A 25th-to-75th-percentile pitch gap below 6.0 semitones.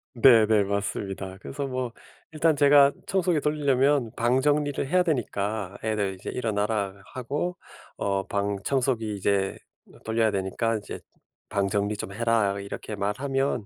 Yes: wide, 5.5 semitones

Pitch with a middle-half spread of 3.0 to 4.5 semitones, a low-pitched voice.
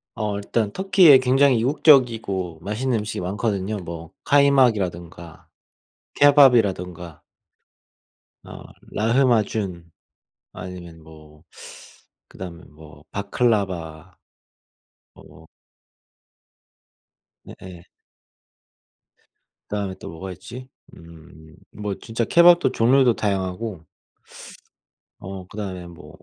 No: wide, 5.6 semitones; low, 100 Hz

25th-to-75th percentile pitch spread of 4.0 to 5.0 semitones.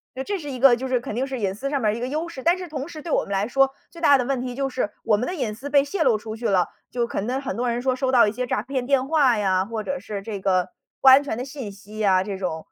Yes: average, 4.5 semitones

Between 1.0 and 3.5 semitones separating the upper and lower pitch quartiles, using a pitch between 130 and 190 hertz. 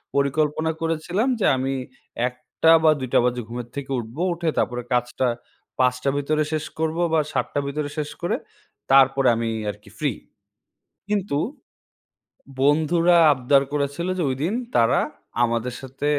No: average, 4.0 semitones; medium, 140 Hz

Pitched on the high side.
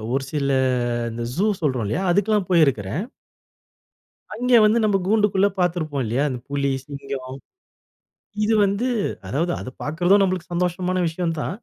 No: medium, 170 Hz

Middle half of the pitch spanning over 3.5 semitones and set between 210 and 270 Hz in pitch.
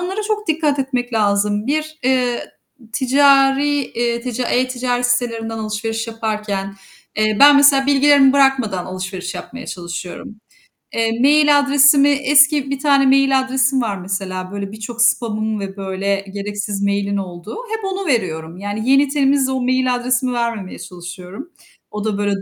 Yes: average, 5.1 semitones; high, 240 Hz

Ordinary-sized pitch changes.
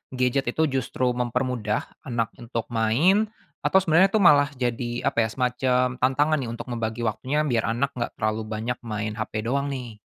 Yes: average, 3.2 semitones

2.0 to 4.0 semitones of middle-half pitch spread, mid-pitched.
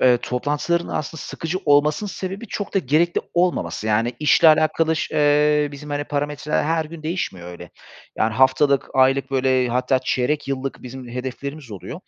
Yes: average, 3.3 semitones; medium, 145 Hz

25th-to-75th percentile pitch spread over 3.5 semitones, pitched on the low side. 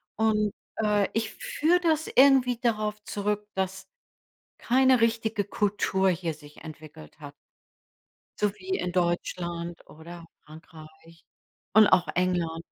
No: average, 4.6 semitones; high, 195 Hz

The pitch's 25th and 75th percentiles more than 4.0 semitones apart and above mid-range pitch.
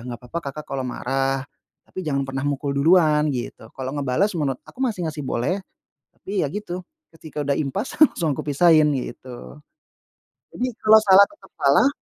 No: average, 5.1 semitones; medium, 150 Hz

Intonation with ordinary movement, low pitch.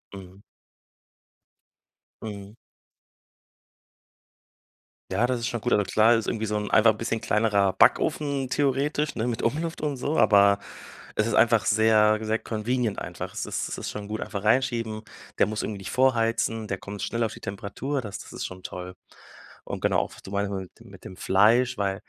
Yes: average, 3.0 semitones; low, 110 Hz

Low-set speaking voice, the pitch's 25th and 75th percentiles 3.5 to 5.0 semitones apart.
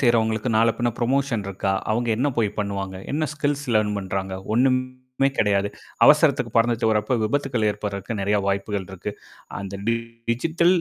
Yes: low, 110 Hz; average, 4.1 semitones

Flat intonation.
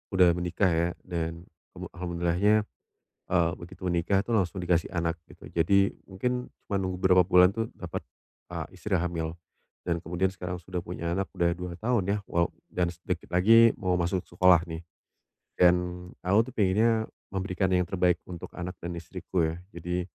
Yes: narrow, 1.9 semitones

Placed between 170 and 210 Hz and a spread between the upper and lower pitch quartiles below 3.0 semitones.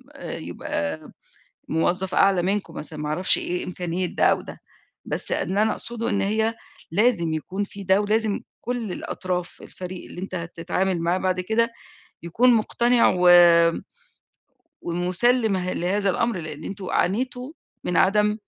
No: high, 190 Hz; average, 3.5 semitones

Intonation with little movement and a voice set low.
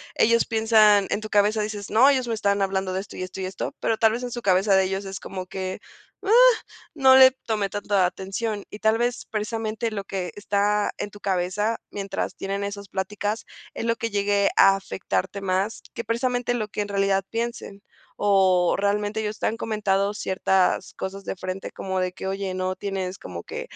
No: narrow, 2.3 semitones; high, 205 Hz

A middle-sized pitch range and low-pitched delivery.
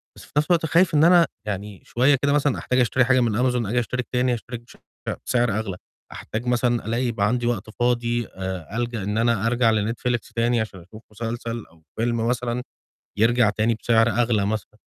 No: narrow, 2.2 semitones; low, 120 Hz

